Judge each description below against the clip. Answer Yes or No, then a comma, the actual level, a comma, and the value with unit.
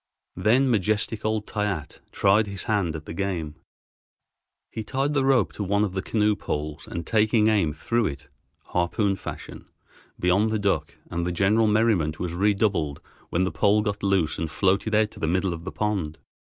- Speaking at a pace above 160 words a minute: Yes, average, 180 wpm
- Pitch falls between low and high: No, low, 100 Hz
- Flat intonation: No, average, 3.9 semitones